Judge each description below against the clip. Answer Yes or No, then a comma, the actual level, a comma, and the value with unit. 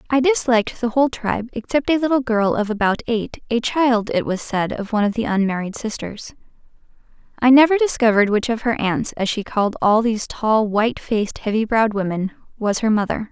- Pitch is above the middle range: Yes, high, 225 Hz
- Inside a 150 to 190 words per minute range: No, average, 200 wpm